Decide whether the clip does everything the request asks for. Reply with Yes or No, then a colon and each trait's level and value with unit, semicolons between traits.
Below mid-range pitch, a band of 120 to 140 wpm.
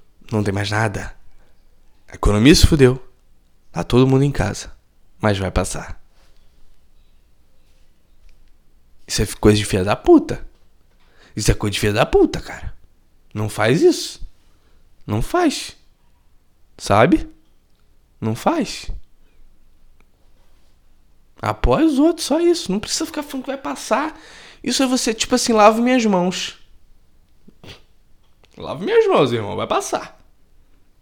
Yes: low, 110 Hz; average, 125 wpm